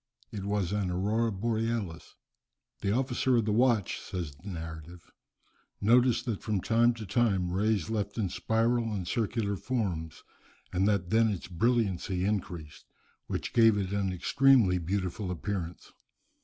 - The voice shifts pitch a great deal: No, average, 3.9 semitones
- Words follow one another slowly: No, average, 145 wpm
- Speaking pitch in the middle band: No, low, 100 Hz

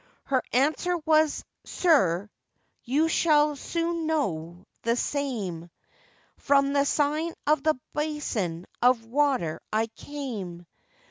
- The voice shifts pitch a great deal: Yes, wide, 6.0 semitones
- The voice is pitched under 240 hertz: No, very high, 280 Hz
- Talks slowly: Yes, slow, 110 wpm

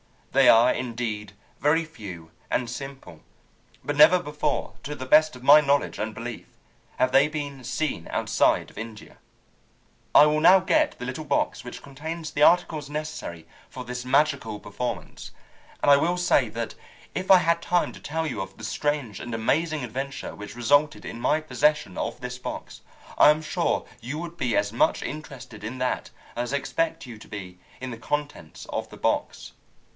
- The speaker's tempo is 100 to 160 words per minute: No, average, 180 wpm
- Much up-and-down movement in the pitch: No, average, 4.7 semitones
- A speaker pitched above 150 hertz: No, low, 135 Hz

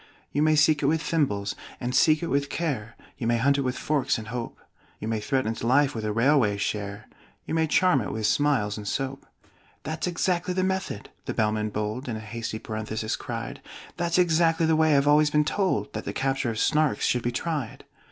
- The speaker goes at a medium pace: No, fast, 220 wpm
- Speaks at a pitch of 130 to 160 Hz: Yes, low, 135 Hz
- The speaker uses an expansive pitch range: Yes, wide, 6.0 semitones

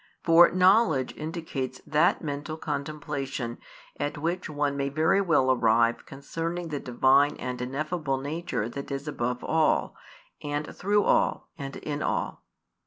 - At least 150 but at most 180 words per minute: No, slow, 135 wpm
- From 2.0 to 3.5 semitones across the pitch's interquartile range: Yes, average, 3.2 semitones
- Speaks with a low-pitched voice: No, medium, 145 Hz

